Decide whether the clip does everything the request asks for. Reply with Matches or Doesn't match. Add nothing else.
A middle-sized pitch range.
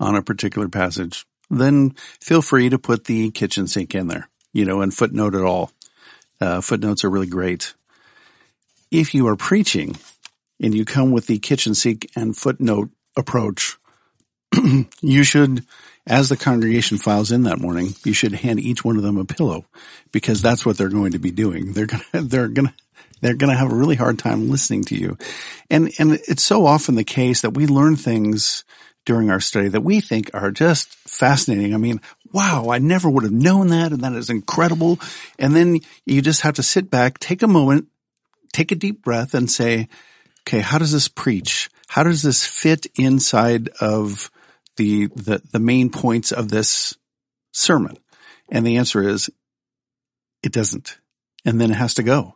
Matches